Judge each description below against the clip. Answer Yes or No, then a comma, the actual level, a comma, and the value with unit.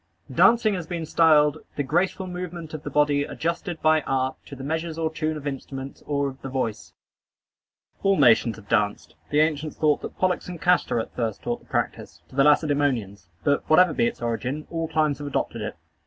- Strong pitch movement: No, average, 3.4 semitones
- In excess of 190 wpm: Yes, average, 200 wpm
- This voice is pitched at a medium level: Yes, medium, 150 Hz